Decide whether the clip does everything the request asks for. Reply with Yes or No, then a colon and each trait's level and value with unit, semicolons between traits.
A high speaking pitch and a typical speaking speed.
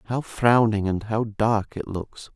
No: low, 110 Hz; average, 180 wpm